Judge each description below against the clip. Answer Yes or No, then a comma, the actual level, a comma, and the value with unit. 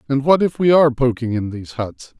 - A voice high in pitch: No, low, 130 Hz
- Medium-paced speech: No, fast, 245 wpm